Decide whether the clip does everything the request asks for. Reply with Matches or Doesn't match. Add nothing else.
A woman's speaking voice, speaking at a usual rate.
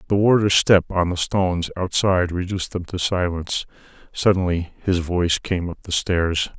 Doesn't match